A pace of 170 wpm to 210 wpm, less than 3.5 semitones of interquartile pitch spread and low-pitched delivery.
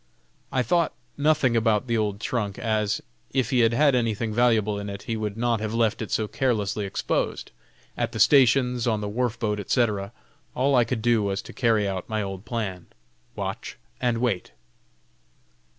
Yes: average, 180 wpm; average, 2.9 semitones; low, 115 Hz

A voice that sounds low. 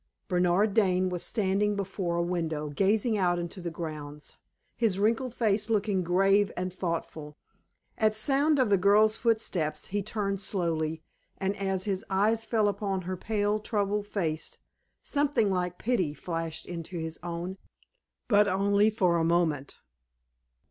No: high, 195 Hz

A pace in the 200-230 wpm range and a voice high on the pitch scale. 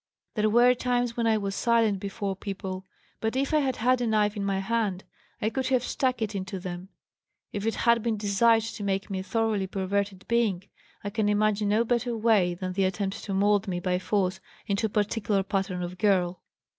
Yes: fast, 205 wpm; high, 205 Hz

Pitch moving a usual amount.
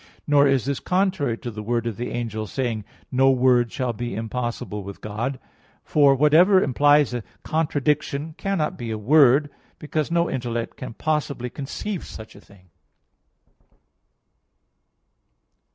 Yes: average, 4.1 semitones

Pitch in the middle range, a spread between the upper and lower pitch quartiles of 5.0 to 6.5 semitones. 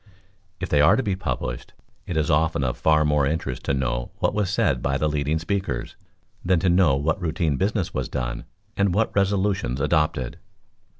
No: very low, 80 Hz; wide, 5.5 semitones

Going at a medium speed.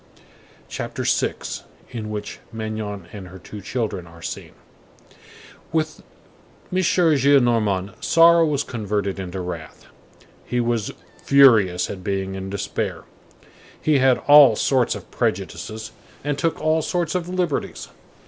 No: slow, 120 wpm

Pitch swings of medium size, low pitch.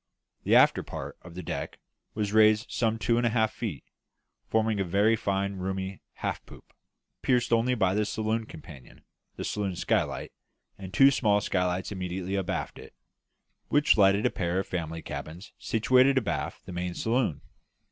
Yes: average, 3.4 semitones; low, 100 Hz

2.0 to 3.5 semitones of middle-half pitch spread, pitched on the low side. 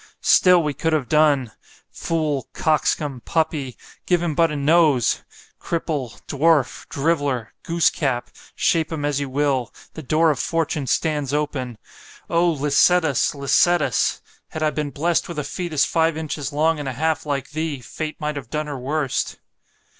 No: narrow, 2.5 semitones; medium, 150 Hz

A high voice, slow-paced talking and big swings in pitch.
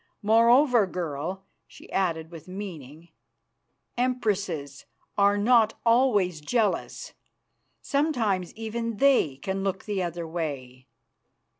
Yes: high, 195 Hz; slow, 100 wpm; wide, 5.7 semitones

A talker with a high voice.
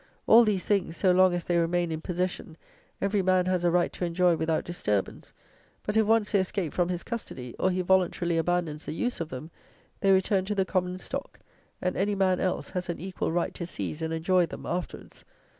No: medium, 180 Hz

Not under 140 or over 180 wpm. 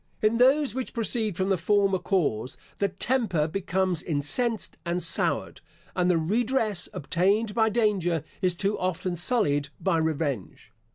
Yes: average, 145 wpm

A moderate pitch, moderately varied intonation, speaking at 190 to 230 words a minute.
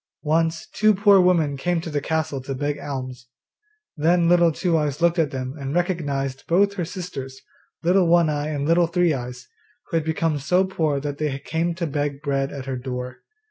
Yes: medium, 155 Hz; average, 3.8 semitones; average, 195 wpm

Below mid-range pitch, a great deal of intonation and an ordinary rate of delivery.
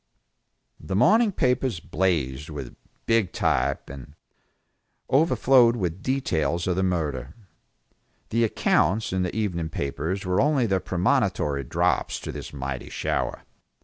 No: very low, 90 Hz; wide, 7.4 semitones; slow, 125 wpm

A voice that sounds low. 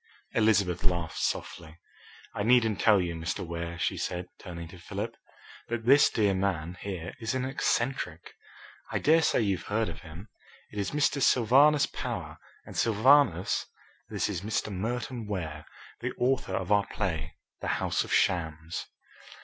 Yes: low, 100 Hz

